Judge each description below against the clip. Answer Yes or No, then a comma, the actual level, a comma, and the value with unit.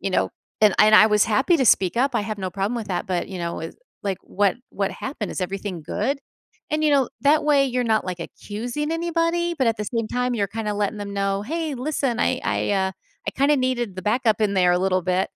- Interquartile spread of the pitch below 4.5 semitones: No, average, 5.2 semitones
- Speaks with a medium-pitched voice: No, high, 215 Hz